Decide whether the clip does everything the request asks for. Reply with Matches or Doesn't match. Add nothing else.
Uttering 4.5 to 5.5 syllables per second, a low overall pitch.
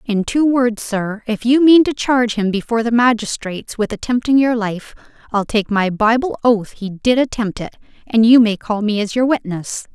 Doesn't match